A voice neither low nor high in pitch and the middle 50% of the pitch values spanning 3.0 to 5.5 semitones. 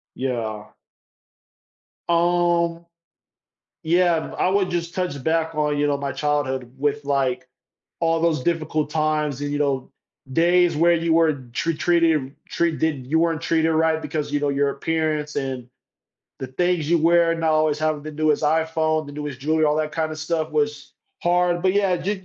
No: medium, 155 Hz; narrow, 2.5 semitones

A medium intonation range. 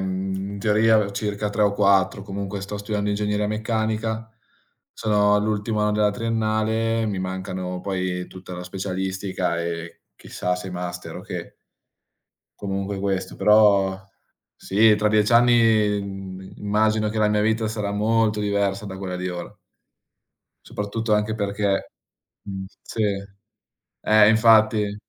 No: narrow, 2.1 semitones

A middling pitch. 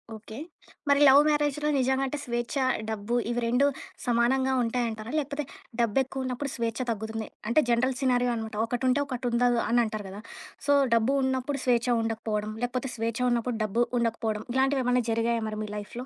No: high, 240 Hz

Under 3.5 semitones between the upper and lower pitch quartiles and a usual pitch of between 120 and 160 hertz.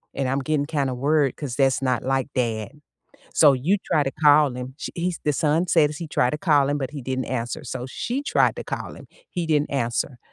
Yes: average, 2.9 semitones; medium, 140 Hz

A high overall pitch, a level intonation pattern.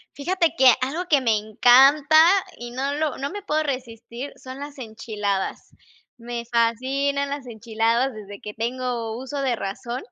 No: very high, 250 Hz; average, 3.5 semitones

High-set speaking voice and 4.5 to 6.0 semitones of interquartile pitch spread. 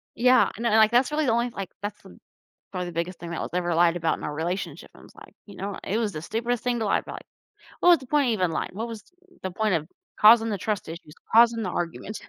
Yes: high, 205 Hz; average, 5.1 semitones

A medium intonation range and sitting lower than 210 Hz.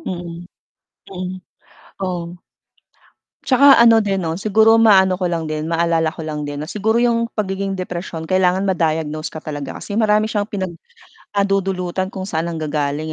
Yes: average, 3.7 semitones; medium, 185 Hz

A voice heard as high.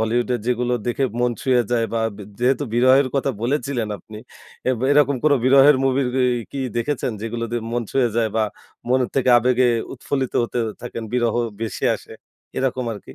No: low, 125 Hz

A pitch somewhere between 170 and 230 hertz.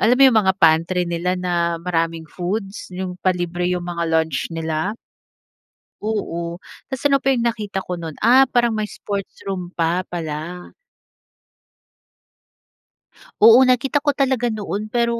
Yes: medium, 185 Hz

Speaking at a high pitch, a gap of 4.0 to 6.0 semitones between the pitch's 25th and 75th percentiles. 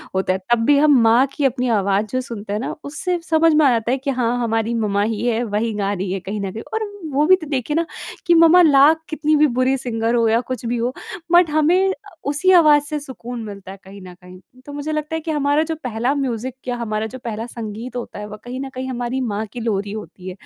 Yes: high, 245 Hz; average, 5.2 semitones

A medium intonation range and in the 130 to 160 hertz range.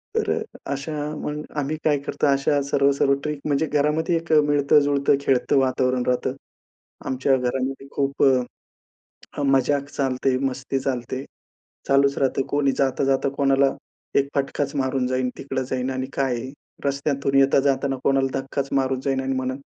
No: narrow, 1.1 semitones; low, 135 Hz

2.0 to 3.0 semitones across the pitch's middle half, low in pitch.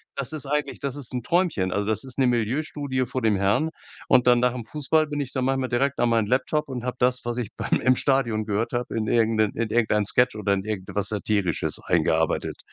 No: average, 3.7 semitones; low, 120 Hz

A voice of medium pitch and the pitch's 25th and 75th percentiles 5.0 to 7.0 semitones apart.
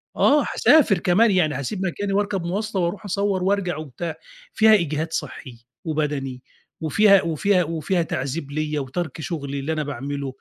Yes: medium, 165 Hz; wide, 5.4 semitones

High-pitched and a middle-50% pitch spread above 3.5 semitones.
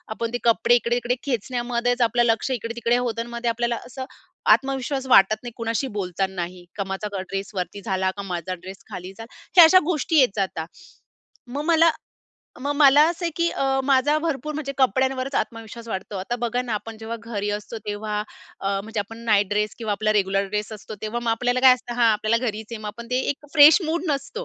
Yes: high, 230 Hz; average, 3.9 semitones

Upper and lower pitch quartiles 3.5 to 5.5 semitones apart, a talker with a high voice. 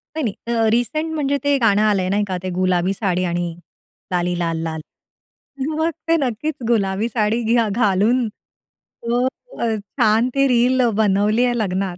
Yes: average, 4.3 semitones; high, 215 Hz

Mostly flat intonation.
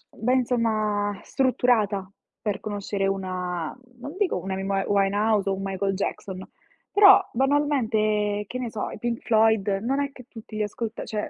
No: average, 3.6 semitones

